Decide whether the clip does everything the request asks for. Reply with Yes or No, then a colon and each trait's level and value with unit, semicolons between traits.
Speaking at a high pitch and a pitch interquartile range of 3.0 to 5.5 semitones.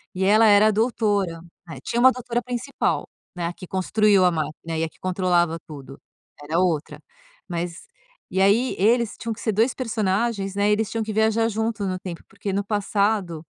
Yes: high, 200 Hz; average, 3.8 semitones